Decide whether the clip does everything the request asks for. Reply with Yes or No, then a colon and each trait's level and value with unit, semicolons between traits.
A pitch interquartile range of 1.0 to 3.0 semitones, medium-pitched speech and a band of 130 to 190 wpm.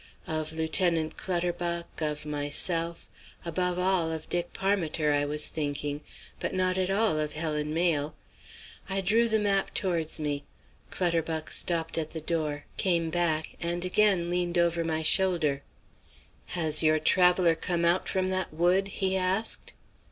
Yes: average, 2.7 semitones; medium, 170 Hz; average, 145 wpm